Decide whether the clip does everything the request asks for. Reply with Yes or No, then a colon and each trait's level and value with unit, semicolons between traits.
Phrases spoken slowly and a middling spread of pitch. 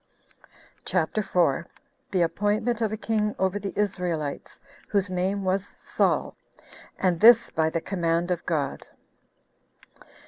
Yes: slow, 125 wpm; average, 3.5 semitones